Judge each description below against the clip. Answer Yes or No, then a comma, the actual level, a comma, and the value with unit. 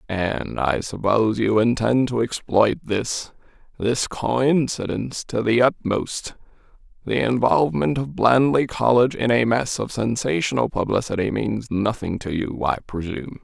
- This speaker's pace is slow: Yes, slow, 125 wpm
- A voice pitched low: Yes, low, 115 Hz